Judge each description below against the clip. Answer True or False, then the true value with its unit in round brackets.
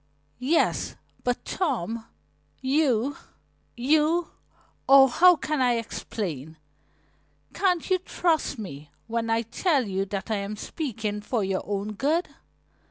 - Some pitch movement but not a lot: False (6.7 semitones)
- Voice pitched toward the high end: True (240 Hz)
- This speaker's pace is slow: True (120 wpm)